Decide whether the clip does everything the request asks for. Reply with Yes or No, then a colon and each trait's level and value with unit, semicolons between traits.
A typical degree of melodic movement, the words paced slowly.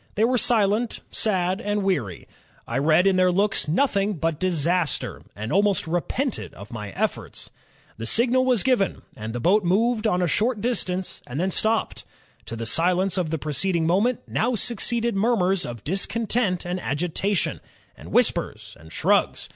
No: average, 4.9 semitones; average, 165 wpm